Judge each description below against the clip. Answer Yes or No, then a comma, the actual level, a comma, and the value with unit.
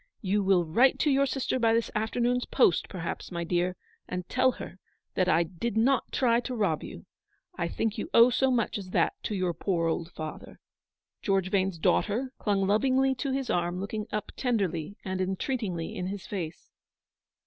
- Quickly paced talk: No, average, 180 wpm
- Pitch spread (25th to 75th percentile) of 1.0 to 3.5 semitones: No, average, 5.2 semitones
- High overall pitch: Yes, high, 200 Hz